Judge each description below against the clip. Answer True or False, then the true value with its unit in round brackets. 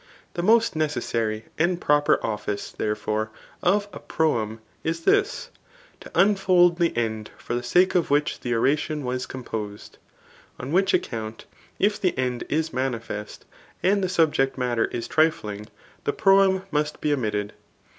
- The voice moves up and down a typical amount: False (7.5 semitones)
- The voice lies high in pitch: False (145 Hz)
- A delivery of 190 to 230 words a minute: False (145 wpm)